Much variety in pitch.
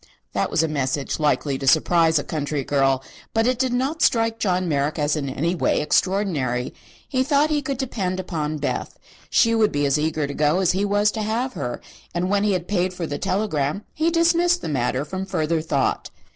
Yes: wide, 6.9 semitones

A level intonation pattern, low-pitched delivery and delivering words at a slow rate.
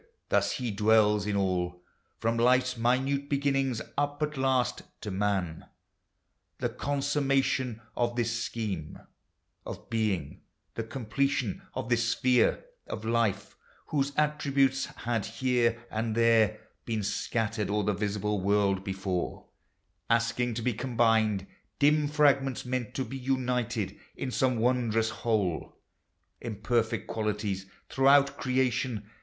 No: average, 3.7 semitones; low, 115 Hz; slow, 125 wpm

